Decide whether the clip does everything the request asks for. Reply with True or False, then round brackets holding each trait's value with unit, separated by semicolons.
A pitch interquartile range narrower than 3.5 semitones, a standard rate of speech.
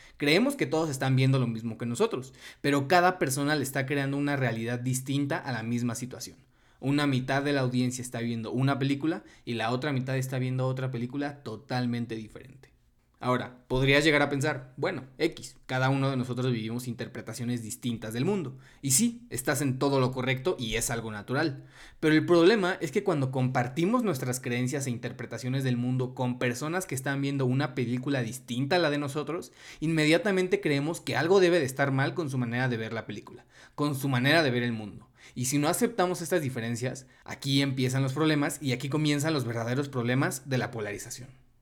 False (2.9 semitones; 195 wpm)